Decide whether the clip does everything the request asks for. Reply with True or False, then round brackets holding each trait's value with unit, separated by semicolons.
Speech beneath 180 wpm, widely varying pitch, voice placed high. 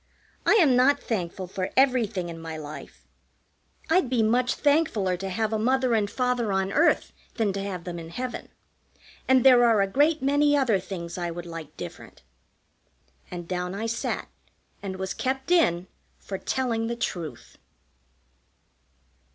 True (160 wpm; 6.2 semitones; 220 Hz)